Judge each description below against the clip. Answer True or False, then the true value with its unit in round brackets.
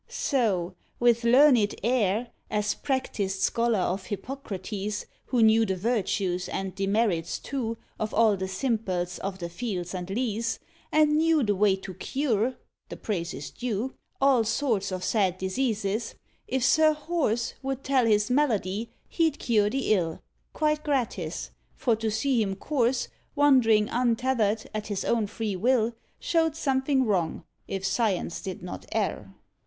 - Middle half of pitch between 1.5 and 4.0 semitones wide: False (5.0 semitones)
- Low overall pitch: False (225 Hz)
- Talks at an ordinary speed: True (150 wpm)